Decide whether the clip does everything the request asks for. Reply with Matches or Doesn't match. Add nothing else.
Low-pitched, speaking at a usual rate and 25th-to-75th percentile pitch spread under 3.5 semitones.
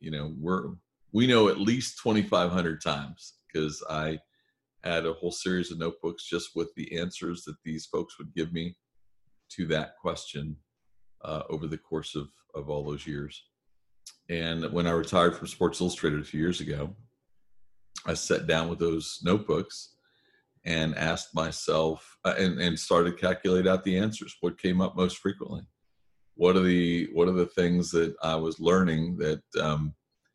Matches